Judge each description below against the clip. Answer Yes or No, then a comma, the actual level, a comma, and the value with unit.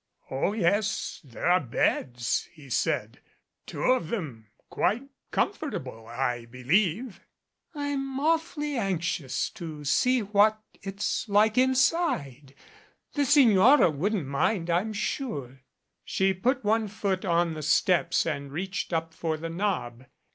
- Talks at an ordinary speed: No, slow, 125 wpm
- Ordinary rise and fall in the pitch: No, wide, 7.5 semitones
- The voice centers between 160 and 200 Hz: Yes, medium, 185 Hz